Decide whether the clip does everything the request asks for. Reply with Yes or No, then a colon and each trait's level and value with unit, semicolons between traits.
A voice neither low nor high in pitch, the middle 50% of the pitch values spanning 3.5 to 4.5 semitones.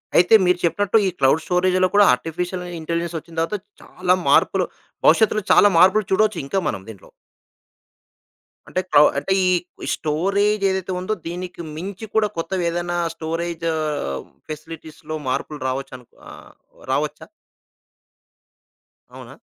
No: medium, 175 Hz; average, 3.1 semitones